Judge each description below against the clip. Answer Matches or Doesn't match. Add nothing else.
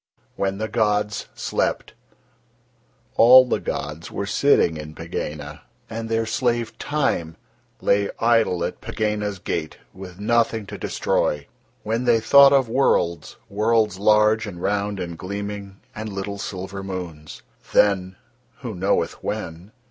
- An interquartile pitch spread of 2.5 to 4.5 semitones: Matches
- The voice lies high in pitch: Doesn't match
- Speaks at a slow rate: Matches